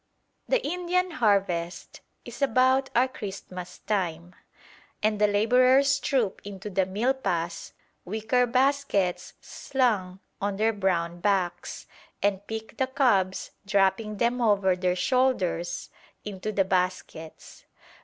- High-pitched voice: Yes, high, 205 Hz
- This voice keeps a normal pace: No, slow, 115 wpm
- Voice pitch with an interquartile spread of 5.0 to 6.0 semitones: Yes, wide, 5.4 semitones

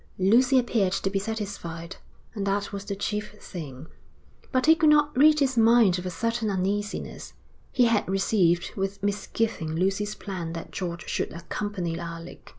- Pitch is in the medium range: No, high, 200 Hz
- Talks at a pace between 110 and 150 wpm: No, average, 160 wpm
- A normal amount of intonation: Yes, average, 3.9 semitones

